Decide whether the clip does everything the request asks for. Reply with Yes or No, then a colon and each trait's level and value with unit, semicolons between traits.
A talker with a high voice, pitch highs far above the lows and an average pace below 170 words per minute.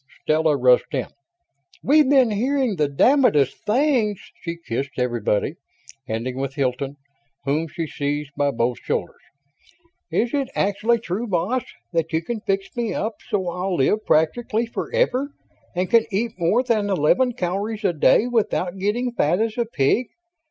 Yes: high, 195 Hz; wide, 8.0 semitones; average, 150 wpm